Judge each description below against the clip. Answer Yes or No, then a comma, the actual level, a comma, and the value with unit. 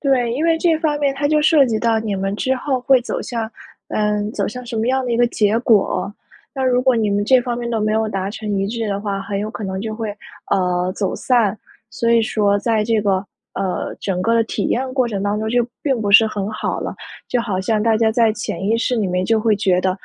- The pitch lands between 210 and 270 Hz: Yes, high, 220 Hz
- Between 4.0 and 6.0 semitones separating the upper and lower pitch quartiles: No, average, 3.2 semitones